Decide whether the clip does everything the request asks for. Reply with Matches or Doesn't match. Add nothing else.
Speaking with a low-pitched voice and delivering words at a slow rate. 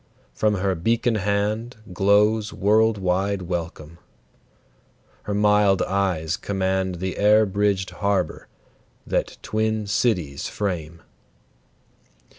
Matches